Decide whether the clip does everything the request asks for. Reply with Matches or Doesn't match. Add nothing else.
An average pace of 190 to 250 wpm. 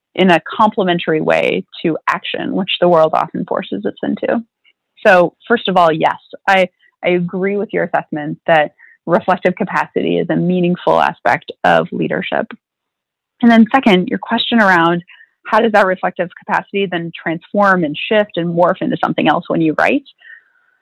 Doesn't match